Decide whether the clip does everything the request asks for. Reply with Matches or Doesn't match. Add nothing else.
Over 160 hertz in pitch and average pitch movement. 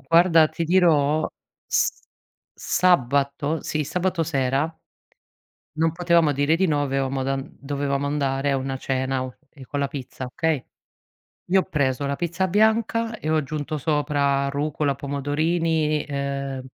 Doesn't match